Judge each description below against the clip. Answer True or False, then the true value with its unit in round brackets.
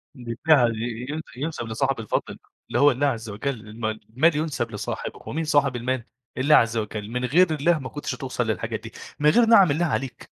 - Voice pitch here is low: True (130 Hz)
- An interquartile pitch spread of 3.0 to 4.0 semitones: False (4.5 semitones)